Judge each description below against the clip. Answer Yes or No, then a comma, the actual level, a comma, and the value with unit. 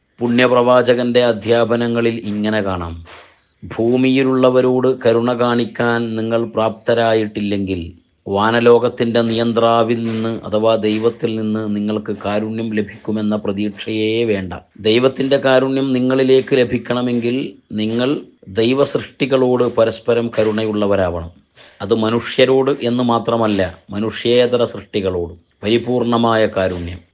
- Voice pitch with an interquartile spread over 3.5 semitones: No, narrow, 2.4 semitones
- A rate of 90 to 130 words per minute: No, average, 80 wpm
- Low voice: Yes, low, 115 Hz